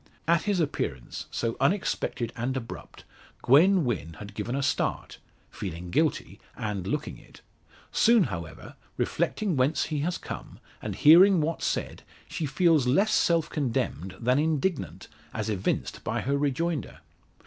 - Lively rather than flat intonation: Yes, wide, 6.5 semitones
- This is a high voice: No, medium, 140 Hz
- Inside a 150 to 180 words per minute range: No, average, 140 wpm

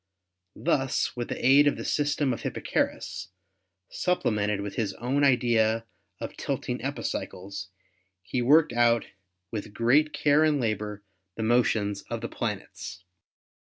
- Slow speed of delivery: Yes, slow, 130 wpm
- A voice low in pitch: Yes, low, 120 Hz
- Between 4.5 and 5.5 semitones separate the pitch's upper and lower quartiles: Yes, average, 5.2 semitones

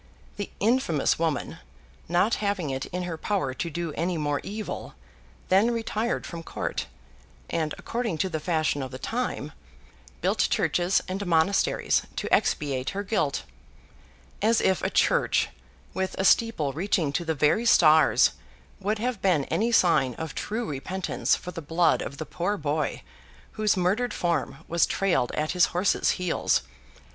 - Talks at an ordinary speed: Yes, average, 155 wpm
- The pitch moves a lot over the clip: No, average, 4.6 semitones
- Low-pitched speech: No, medium, 175 Hz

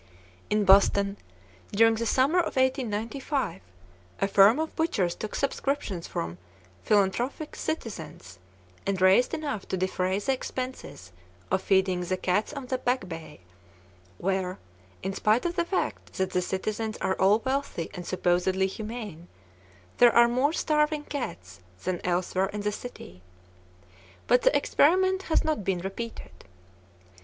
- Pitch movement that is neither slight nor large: No, wide, 5.9 semitones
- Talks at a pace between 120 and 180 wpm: Yes, average, 140 wpm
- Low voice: No, high, 210 Hz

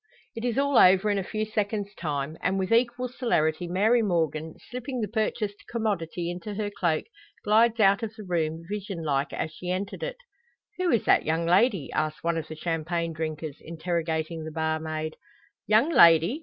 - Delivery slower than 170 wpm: No, average, 180 wpm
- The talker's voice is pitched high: No, medium, 180 Hz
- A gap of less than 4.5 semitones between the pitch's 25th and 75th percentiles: No, average, 5.2 semitones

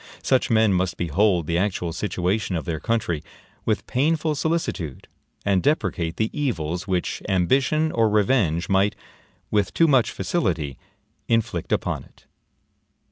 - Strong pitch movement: Yes, wide, 6.2 semitones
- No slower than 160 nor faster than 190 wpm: No, slow, 135 wpm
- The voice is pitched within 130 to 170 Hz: No, low, 100 Hz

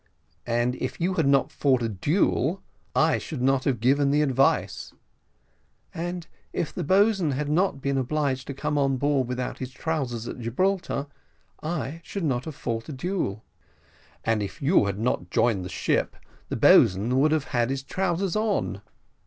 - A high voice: No, medium, 140 Hz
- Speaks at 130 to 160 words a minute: No, average, 170 wpm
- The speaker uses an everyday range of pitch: Yes, average, 4.5 semitones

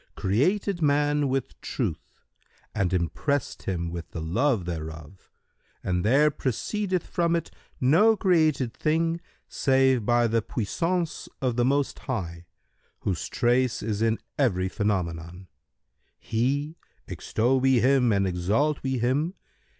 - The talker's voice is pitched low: Yes, low, 125 Hz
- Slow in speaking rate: Yes, slow, 125 wpm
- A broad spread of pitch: Yes, wide, 7.2 semitones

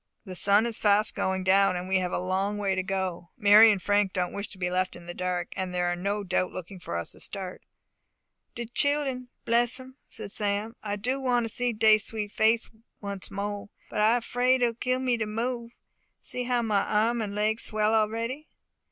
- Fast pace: Yes, fast, 215 wpm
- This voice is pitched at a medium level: No, high, 210 Hz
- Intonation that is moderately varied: Yes, average, 3.7 semitones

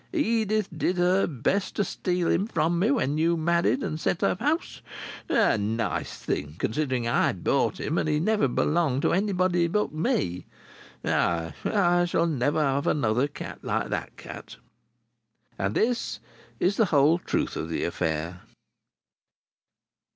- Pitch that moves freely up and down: Yes, wide, 6.7 semitones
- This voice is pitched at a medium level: Yes, medium, 165 Hz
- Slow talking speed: No, average, 150 wpm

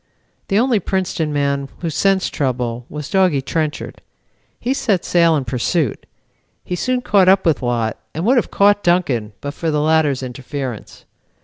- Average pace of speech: Yes, average, 165 wpm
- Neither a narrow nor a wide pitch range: No, wide, 5.9 semitones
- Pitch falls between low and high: Yes, medium, 155 Hz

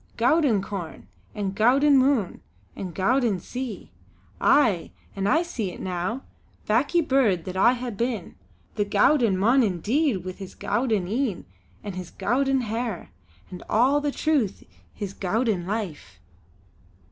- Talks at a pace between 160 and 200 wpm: No, average, 140 wpm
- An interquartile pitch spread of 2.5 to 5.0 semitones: No, wide, 5.5 semitones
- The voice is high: Yes, high, 220 Hz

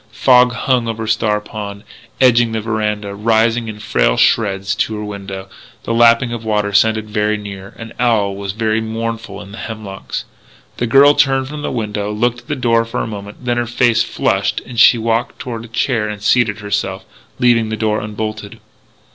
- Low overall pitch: Yes, low, 110 Hz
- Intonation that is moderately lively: No, narrow, 2.1 semitones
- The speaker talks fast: No, average, 190 wpm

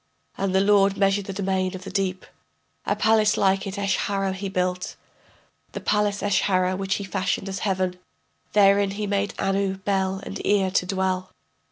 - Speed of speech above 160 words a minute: Yes, average, 170 wpm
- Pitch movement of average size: No, narrow, 1.0 semitones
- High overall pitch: Yes, high, 195 Hz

